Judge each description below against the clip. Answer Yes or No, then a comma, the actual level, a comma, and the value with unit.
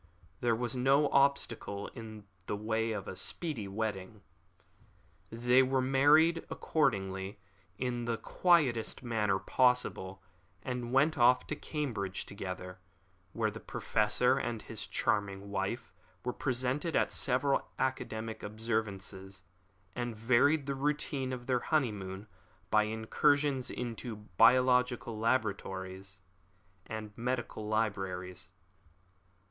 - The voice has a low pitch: Yes, low, 115 Hz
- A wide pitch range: No, average, 4.1 semitones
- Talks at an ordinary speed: No, slow, 110 wpm